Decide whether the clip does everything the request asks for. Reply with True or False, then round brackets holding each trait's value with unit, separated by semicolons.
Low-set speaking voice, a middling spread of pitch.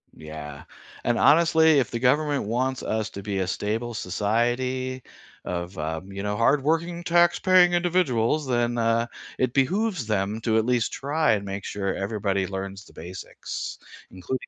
False (115 Hz; 6.3 semitones)